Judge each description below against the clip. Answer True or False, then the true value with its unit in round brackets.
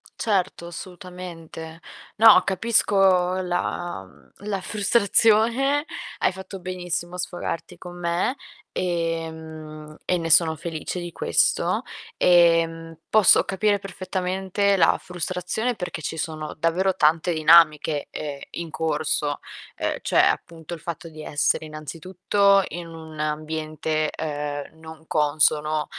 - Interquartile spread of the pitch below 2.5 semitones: False (2.8 semitones)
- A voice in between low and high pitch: True (170 Hz)